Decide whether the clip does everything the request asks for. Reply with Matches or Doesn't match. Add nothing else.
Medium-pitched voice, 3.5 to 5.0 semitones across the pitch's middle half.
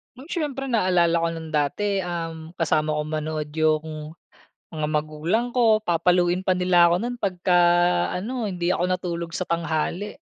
Doesn't match